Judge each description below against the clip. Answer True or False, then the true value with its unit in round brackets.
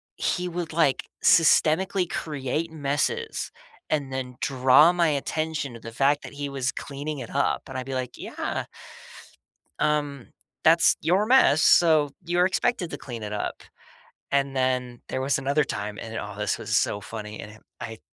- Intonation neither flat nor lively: True (4.1 semitones)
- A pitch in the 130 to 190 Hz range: True (140 Hz)